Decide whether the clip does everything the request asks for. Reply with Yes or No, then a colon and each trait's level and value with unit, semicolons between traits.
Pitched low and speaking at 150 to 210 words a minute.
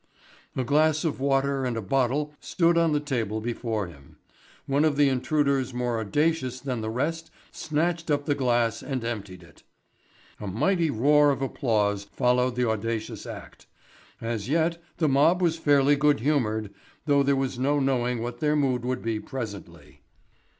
Yes: low, 130 Hz; average, 165 wpm